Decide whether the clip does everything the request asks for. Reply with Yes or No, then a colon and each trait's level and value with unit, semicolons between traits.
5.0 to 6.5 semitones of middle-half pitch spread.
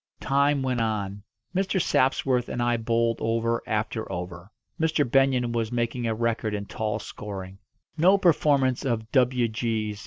No: average, 3.2 semitones